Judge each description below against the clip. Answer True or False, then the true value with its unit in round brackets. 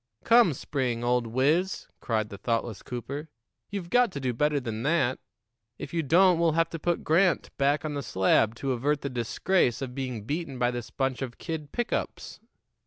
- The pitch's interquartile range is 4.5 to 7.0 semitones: True (5.2 semitones)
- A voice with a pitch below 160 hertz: True (140 Hz)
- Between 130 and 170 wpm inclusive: False (190 wpm)